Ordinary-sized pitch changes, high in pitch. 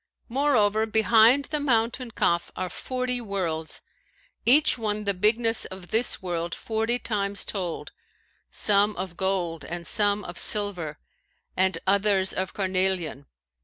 Yes: average, 3.5 semitones; high, 205 Hz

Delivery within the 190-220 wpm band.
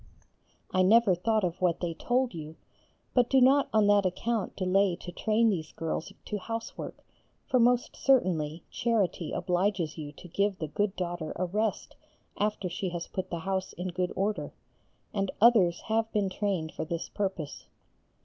No: average, 170 wpm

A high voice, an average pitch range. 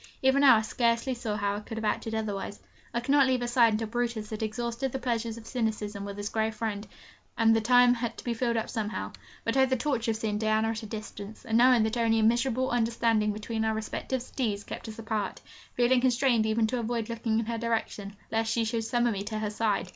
No: high, 225 Hz; narrow, 1.8 semitones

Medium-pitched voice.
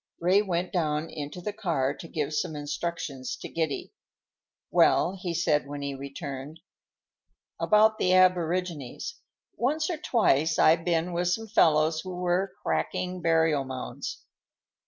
Yes: medium, 165 Hz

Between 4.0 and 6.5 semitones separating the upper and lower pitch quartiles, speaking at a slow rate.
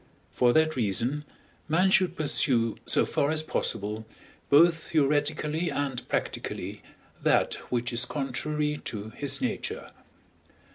Yes: average, 4.4 semitones; slow, 115 wpm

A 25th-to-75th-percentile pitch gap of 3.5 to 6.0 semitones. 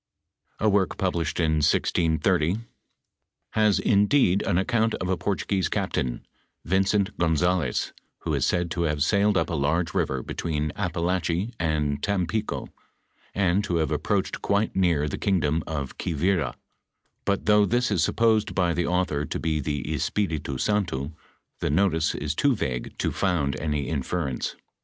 Yes: average, 4.6 semitones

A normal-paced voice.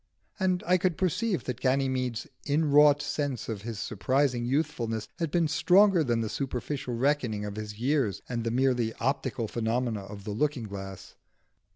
Yes: average, 160 wpm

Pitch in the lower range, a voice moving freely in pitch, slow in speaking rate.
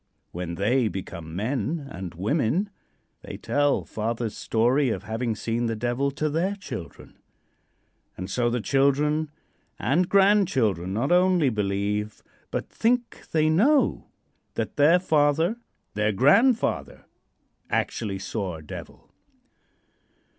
Yes: low, 125 Hz; wide, 7.0 semitones; slow, 120 wpm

